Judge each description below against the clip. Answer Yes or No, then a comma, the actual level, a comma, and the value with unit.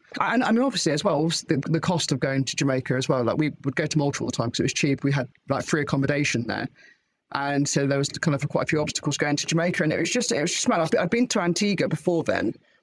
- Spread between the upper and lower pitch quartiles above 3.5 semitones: No, average, 3.2 semitones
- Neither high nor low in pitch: Yes, medium, 150 Hz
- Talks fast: Yes, fast, 285 wpm